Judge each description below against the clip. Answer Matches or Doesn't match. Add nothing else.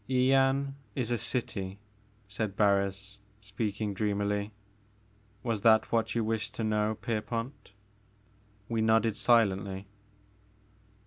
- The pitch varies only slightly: Matches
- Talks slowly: Matches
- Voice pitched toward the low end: Matches